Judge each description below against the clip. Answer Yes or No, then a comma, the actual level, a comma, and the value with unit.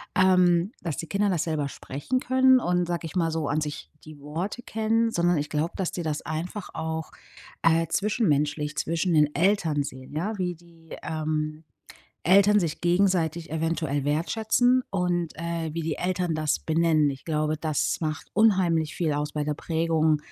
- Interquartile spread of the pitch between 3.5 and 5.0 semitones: No, average, 2.9 semitones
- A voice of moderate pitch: Yes, medium, 165 Hz